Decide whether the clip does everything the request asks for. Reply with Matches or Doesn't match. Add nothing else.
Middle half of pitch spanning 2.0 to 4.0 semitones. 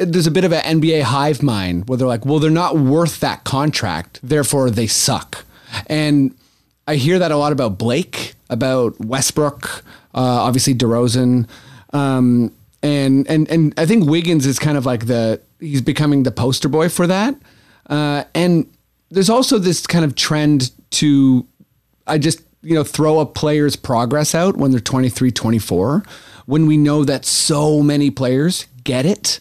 Matches